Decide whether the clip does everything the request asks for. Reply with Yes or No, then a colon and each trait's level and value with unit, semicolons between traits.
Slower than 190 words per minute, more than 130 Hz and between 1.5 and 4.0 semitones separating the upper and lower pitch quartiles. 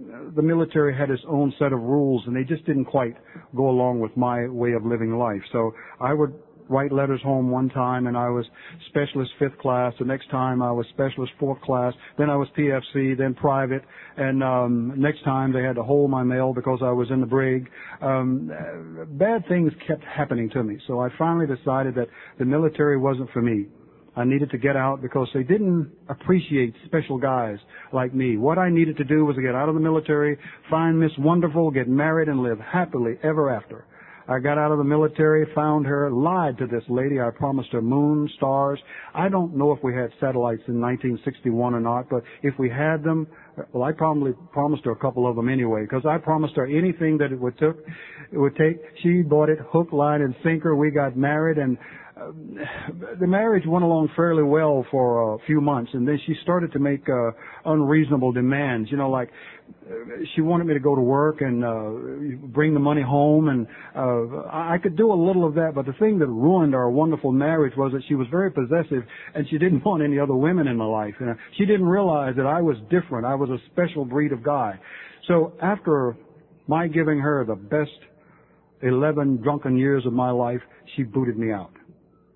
No: fast, 205 wpm; medium, 140 Hz; average, 3.4 semitones